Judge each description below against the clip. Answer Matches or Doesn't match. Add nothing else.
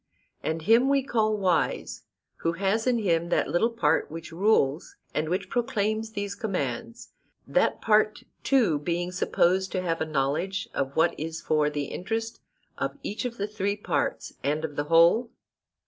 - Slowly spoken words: Doesn't match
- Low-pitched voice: Doesn't match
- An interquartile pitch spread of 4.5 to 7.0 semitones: Matches